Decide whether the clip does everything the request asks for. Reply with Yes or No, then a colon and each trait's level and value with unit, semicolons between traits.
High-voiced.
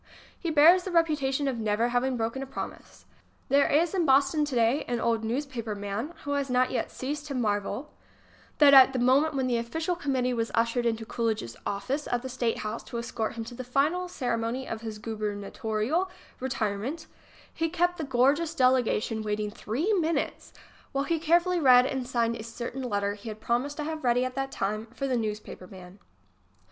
Yes: very high, 255 Hz